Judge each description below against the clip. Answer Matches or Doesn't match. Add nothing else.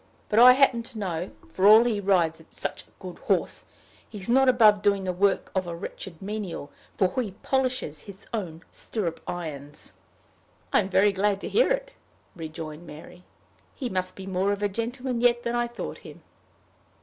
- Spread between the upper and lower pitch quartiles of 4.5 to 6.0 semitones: Matches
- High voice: Matches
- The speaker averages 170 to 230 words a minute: Matches